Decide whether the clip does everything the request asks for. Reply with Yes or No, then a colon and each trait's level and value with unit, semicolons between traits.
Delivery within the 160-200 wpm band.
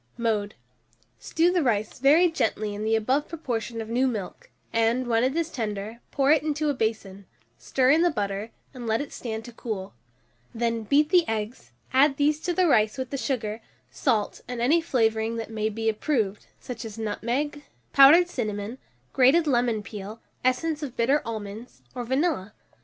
Yes: average, 175 wpm